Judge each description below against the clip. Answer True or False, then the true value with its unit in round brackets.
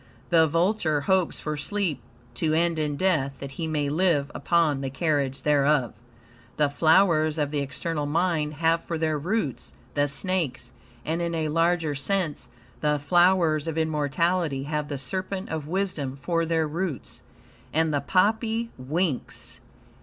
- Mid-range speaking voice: True (155 Hz)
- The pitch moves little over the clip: False (3.0 semitones)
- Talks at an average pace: True (150 wpm)